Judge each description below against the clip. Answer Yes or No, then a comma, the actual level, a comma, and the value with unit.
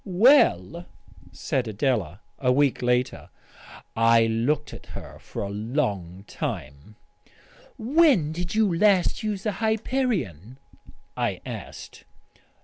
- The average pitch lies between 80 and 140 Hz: Yes, low, 135 Hz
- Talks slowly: Yes, slow, 110 wpm